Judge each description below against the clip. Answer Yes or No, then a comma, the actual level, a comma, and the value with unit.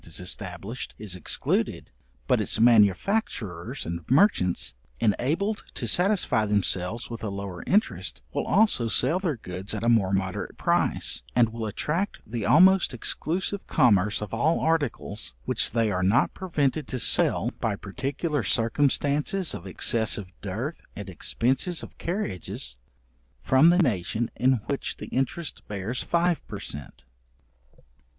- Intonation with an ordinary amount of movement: No, wide, 7.8 semitones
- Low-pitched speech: Yes, low, 115 Hz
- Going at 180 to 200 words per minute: No, average, 140 wpm